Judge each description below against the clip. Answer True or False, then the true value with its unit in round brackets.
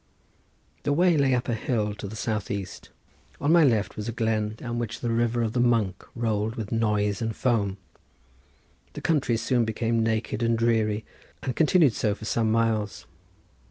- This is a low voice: True (115 Hz)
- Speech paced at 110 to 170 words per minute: False (180 wpm)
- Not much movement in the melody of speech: True (2.0 semitones)